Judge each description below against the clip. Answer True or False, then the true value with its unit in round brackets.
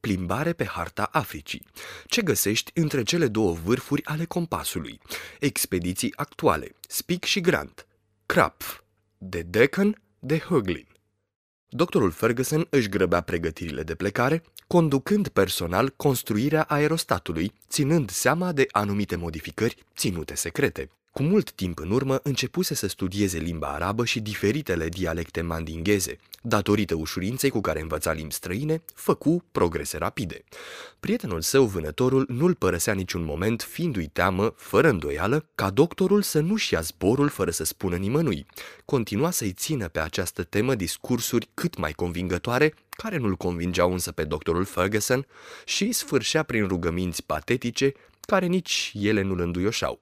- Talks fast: False (135 wpm)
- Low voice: True (110 Hz)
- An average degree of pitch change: False (8.9 semitones)